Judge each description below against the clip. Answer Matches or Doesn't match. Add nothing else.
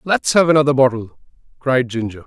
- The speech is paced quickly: Doesn't match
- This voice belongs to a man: Matches